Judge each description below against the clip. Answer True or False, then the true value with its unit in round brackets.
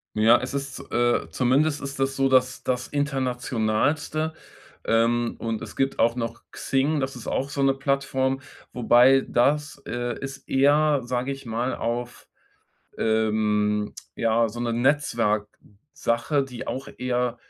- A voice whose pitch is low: True (125 Hz)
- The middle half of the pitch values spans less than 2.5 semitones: False (2.8 semitones)